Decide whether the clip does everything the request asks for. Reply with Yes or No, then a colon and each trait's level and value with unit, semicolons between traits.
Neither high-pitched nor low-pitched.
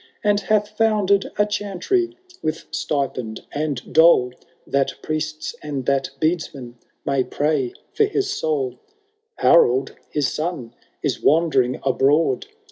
Yes: medium, 155 Hz